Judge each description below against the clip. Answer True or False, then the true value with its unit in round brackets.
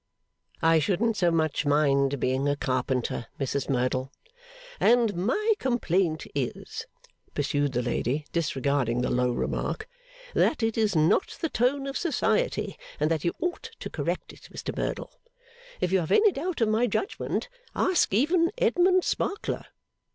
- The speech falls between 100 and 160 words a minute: True (150 wpm)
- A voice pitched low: False (170 Hz)